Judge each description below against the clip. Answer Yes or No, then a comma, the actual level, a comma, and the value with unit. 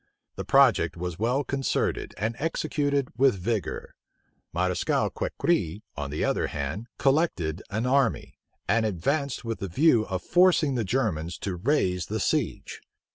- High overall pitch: No, low, 110 Hz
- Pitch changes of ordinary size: No, wide, 7.3 semitones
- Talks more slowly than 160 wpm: Yes, average, 140 wpm